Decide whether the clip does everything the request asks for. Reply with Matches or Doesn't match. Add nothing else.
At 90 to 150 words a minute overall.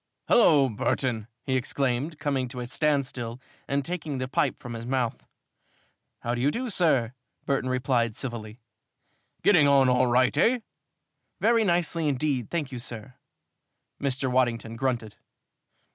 Matches